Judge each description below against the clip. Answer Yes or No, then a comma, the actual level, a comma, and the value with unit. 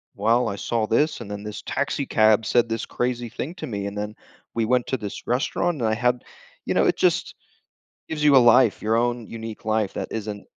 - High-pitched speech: No, low, 115 Hz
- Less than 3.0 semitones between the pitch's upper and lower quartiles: Yes, narrow, 2.4 semitones